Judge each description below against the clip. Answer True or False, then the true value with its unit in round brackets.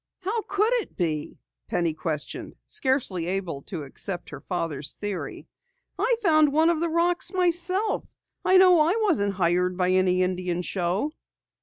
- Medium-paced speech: True (150 wpm)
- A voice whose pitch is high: True (200 Hz)